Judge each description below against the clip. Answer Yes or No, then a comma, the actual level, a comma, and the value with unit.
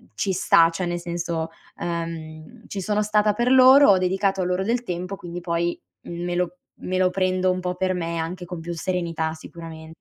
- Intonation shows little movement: Yes, narrow, 2.1 semitones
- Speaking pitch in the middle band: Yes, medium, 180 Hz